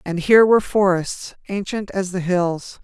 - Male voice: No, female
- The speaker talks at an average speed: Yes, average, 170 wpm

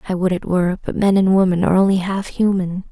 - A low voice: No, medium, 185 Hz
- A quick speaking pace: Yes, fast, 245 wpm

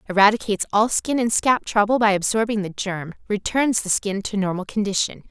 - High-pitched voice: Yes, high, 210 Hz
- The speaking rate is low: No, average, 170 wpm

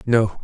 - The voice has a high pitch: No, low, 110 Hz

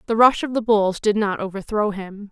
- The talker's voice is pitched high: Yes, high, 210 Hz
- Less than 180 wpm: No, fast, 235 wpm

